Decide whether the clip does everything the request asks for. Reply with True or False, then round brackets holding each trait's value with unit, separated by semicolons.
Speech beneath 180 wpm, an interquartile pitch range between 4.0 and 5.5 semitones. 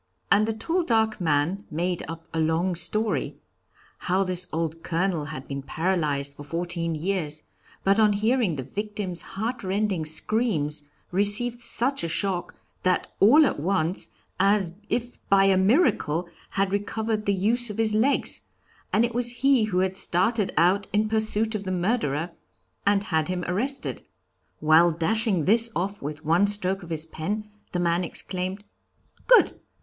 True (155 wpm; 4.5 semitones)